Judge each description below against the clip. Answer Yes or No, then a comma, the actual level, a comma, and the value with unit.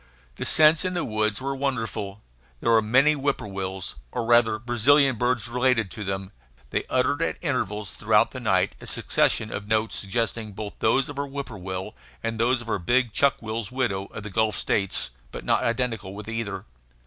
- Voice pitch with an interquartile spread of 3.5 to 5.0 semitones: Yes, average, 3.8 semitones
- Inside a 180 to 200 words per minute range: Yes, average, 185 wpm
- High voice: No, low, 115 Hz